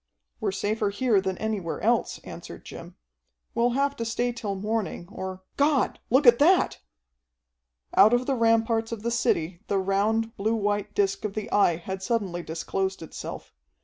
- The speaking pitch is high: Yes, high, 215 Hz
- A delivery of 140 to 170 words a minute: Yes, average, 165 wpm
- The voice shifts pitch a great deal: No, average, 3.3 semitones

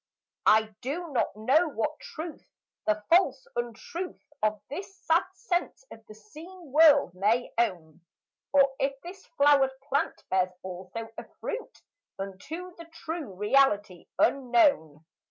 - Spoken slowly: Yes, slow, 130 wpm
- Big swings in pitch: Yes, wide, 7.4 semitones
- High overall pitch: Yes, very high, 270 Hz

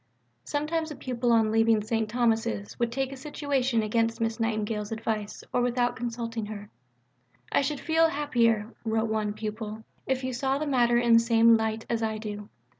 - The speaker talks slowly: No, average, 180 wpm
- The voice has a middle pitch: No, high, 230 Hz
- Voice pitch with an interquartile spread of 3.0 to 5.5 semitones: No, narrow, 2.4 semitones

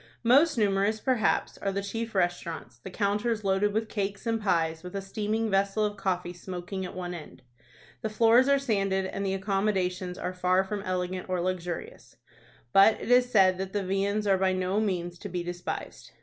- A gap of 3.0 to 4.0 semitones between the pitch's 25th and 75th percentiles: No, narrow, 2.6 semitones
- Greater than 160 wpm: Yes, average, 190 wpm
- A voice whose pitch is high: Yes, high, 195 Hz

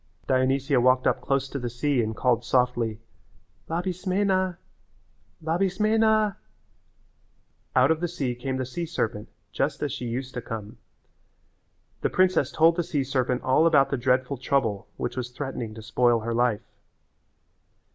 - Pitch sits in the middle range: No, low, 130 Hz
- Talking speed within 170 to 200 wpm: No, average, 145 wpm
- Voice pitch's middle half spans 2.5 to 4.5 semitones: No, average, 5.2 semitones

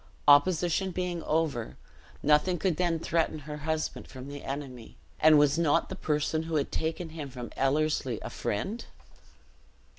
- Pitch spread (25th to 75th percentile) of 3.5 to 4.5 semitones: No, narrow, 2.6 semitones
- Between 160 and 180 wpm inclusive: No, average, 150 wpm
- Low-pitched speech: No, medium, 155 Hz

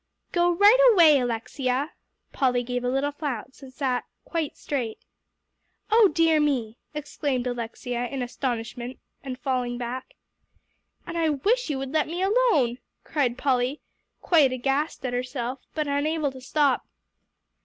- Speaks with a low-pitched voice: No, very high, 270 Hz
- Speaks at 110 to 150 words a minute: Yes, average, 140 wpm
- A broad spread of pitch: No, average, 3.7 semitones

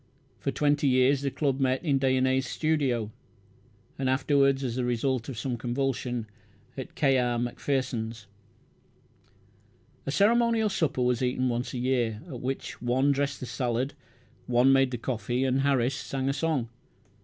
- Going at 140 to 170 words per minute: Yes, average, 155 wpm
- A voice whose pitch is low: Yes, low, 130 Hz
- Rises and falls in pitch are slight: Yes, narrow, 2.0 semitones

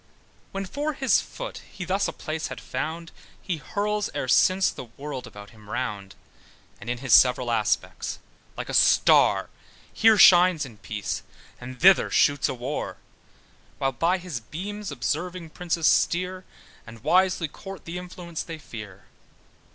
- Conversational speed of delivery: Yes, average, 150 wpm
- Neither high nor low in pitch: Yes, medium, 165 Hz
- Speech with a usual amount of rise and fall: No, wide, 6.8 semitones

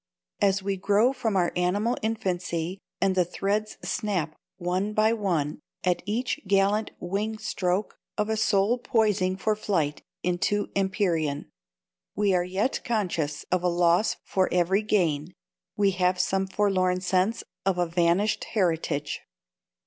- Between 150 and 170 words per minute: No, average, 140 wpm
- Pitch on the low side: No, high, 190 Hz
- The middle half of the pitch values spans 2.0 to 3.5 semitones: Yes, average, 2.8 semitones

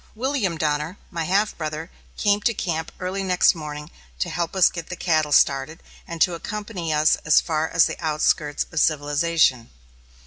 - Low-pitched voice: No, medium, 165 Hz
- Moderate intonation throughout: Yes, average, 3.2 semitones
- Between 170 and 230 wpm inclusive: Yes, average, 175 wpm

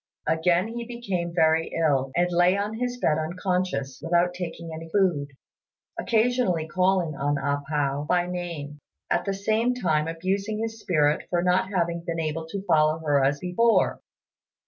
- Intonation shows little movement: No, average, 3.8 semitones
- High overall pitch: No, medium, 175 Hz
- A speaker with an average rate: Yes, average, 160 wpm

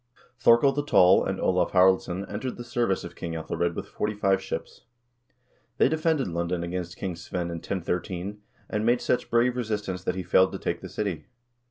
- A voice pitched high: No, very low, 95 Hz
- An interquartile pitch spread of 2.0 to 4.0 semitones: No, average, 4.8 semitones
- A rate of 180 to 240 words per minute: Yes, average, 185 wpm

